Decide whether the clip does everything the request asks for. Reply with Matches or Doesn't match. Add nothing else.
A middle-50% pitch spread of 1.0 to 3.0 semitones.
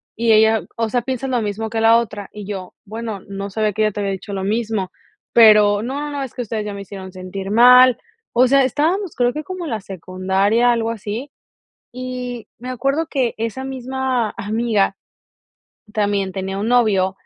Doesn't match